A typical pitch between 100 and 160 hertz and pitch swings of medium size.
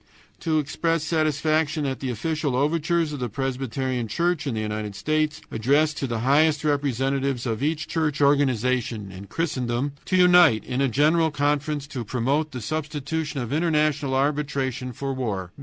Yes: medium, 140 Hz; average, 3.5 semitones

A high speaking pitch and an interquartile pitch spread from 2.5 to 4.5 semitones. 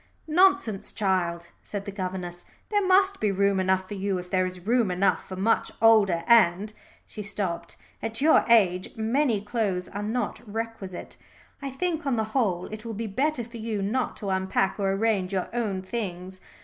Yes: high, 205 Hz; average, 3.5 semitones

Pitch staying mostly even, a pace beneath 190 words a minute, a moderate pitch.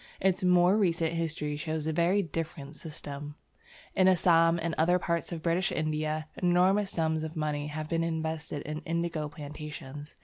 Yes: narrow, 2.0 semitones; average, 160 wpm; medium, 160 Hz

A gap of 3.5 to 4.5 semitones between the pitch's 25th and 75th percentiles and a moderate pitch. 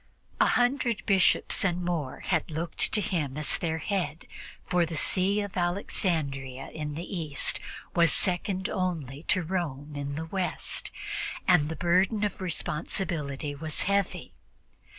Yes: average, 3.9 semitones; medium, 170 Hz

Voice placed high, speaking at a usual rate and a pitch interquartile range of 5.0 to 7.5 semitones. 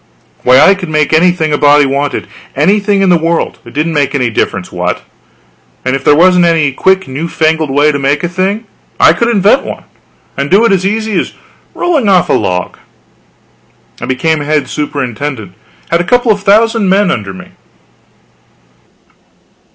No: medium, 160 Hz; average, 175 wpm; wide, 5.4 semitones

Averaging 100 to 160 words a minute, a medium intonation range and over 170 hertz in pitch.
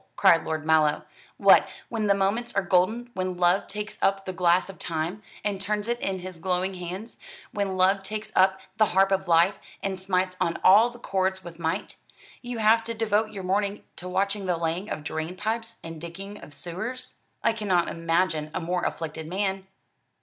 No: average, 190 wpm; average, 3.0 semitones; high, 190 Hz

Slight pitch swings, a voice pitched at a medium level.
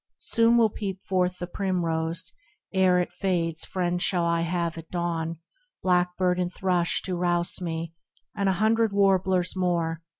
Yes: narrow, 1.9 semitones; medium, 180 Hz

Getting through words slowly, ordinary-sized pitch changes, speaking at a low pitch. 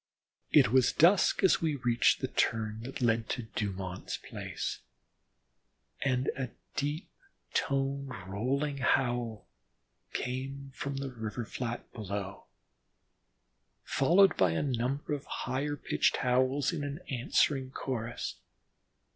Yes: slow, 115 wpm; average, 3.2 semitones; low, 130 Hz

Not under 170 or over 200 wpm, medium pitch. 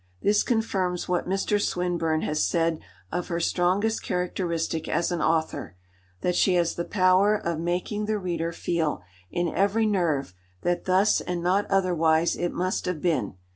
No: average, 160 wpm; medium, 175 Hz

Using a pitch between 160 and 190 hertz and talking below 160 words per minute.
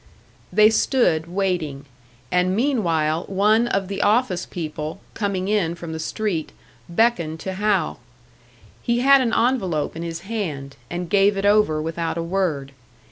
Yes: medium, 185 Hz; average, 145 wpm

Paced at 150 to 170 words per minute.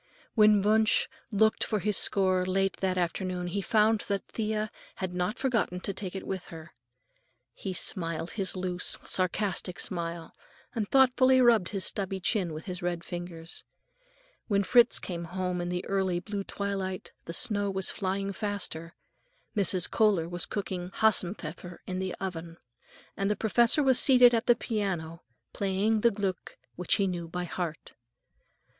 Yes: average, 155 wpm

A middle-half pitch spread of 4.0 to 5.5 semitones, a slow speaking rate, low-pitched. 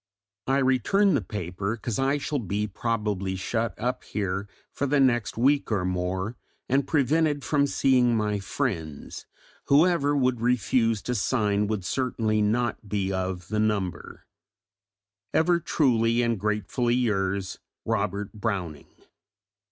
Yes: average, 4.6 semitones; slow, 130 wpm; low, 110 Hz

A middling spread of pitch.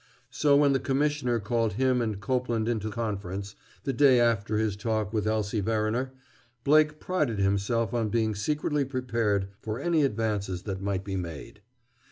Yes: average, 4.2 semitones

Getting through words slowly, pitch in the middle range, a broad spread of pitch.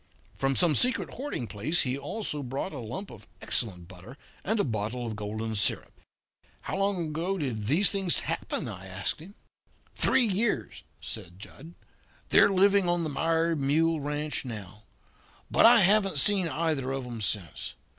No: average, 160 wpm; medium, 145 Hz; wide, 8.4 semitones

